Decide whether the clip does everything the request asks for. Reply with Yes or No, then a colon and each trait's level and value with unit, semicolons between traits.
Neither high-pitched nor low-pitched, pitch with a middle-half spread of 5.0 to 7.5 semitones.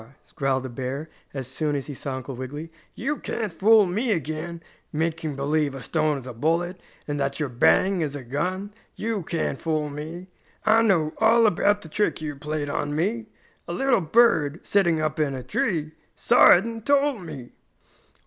Yes: medium, 155 Hz; wide, 5.5 semitones